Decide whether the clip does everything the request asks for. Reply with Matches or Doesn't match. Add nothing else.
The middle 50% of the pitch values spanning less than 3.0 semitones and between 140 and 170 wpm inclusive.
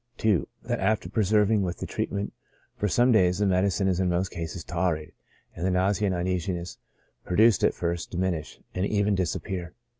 Doesn't match